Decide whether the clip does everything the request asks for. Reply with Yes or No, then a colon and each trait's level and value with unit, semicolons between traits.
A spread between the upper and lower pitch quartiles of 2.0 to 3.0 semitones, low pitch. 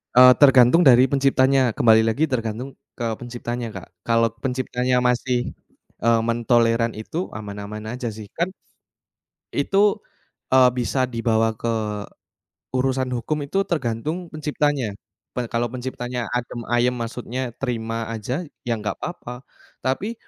Yes: narrow, 2.4 semitones; low, 125 Hz